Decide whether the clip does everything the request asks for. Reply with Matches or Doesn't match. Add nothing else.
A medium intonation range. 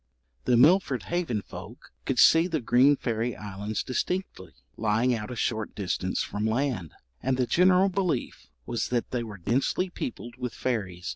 Matches